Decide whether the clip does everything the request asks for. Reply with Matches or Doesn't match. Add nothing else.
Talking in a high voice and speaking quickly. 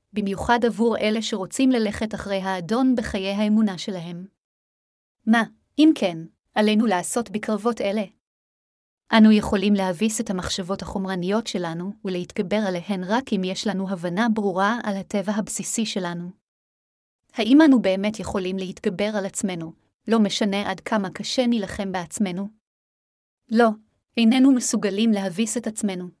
Doesn't match